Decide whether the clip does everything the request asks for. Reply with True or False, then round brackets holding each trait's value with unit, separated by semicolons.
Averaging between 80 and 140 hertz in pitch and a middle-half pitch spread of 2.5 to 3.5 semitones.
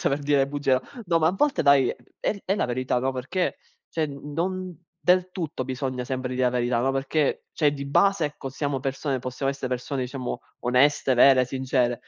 True (135 Hz; 2.9 semitones)